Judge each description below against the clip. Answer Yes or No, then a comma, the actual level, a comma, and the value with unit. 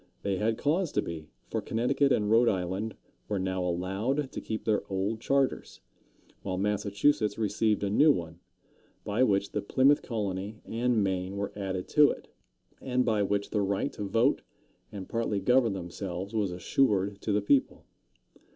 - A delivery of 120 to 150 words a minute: No, average, 165 wpm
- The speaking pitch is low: Yes, low, 105 Hz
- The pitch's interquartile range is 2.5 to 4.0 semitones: Yes, average, 3.3 semitones